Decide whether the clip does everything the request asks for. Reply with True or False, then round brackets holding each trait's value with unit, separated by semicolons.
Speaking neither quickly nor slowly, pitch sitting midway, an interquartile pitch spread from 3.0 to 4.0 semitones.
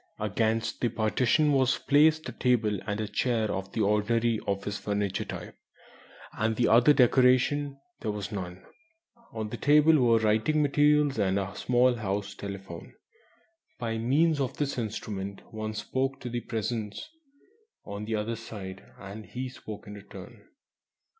False (145 wpm; 110 Hz; 3.6 semitones)